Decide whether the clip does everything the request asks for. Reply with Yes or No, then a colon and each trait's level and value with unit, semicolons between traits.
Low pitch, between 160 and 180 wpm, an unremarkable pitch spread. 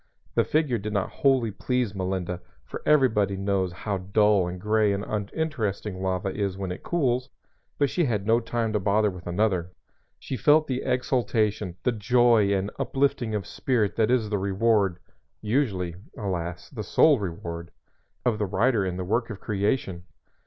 Yes: low, 105 Hz; average, 165 wpm; average, 4.0 semitones